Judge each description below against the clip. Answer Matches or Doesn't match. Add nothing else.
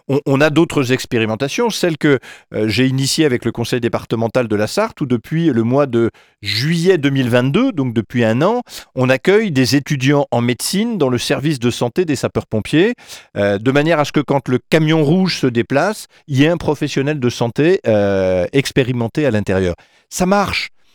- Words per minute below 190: Matches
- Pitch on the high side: Doesn't match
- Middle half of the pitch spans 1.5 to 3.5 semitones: Doesn't match